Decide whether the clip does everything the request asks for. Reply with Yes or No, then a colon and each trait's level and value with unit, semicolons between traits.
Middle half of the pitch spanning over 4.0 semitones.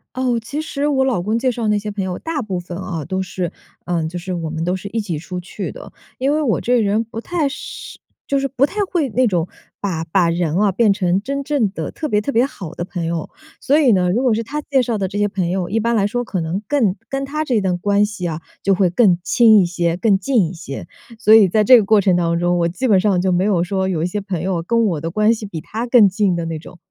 Yes: average, 4.9 semitones